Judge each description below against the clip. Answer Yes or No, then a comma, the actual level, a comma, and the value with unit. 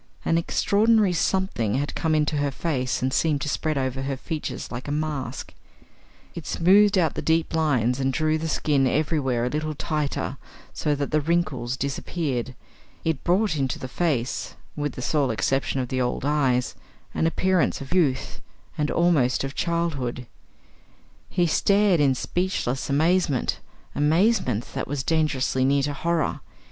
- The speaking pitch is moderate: Yes, medium, 150 Hz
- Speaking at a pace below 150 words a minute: No, average, 155 wpm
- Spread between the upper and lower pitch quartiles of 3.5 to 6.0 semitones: Yes, average, 4.0 semitones